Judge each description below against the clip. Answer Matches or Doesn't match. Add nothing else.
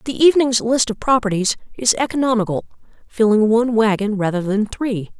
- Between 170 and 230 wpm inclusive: Doesn't match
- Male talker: Doesn't match